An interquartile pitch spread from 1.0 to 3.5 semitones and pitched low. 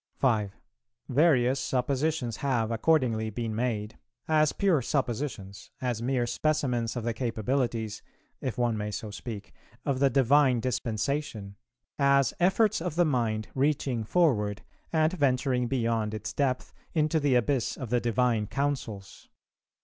No: average, 4.0 semitones; low, 125 Hz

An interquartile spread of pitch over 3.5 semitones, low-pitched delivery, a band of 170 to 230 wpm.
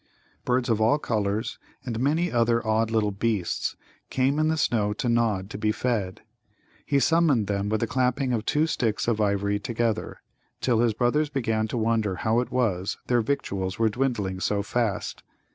No: average, 3.2 semitones; low, 115 Hz; average, 180 wpm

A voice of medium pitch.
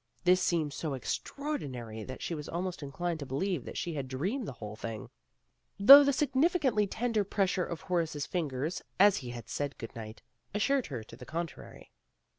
Yes: medium, 170 Hz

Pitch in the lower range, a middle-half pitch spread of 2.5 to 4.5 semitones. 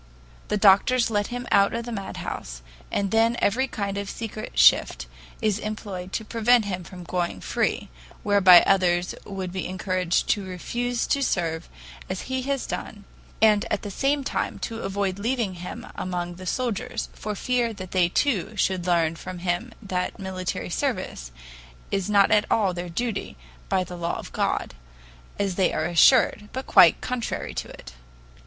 No: high, 200 Hz; average, 3.8 semitones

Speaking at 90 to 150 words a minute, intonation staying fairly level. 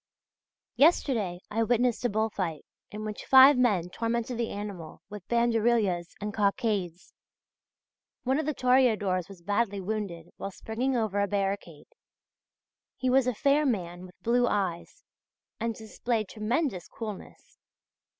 No: slow, 135 wpm; average, 3.8 semitones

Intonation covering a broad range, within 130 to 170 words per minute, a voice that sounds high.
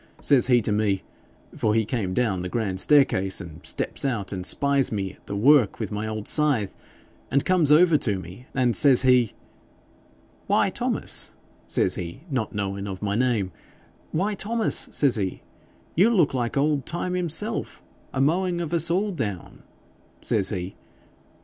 No: wide, 7.1 semitones; average, 165 wpm; low, 120 Hz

